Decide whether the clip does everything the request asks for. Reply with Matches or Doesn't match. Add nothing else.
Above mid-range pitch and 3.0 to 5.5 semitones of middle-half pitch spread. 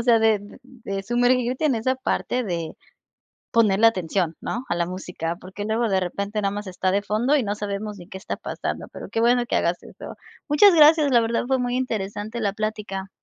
Matches